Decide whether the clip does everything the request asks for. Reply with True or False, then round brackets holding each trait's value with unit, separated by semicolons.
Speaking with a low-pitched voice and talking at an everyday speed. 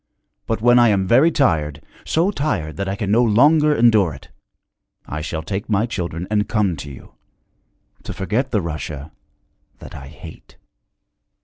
True (105 Hz; 165 wpm)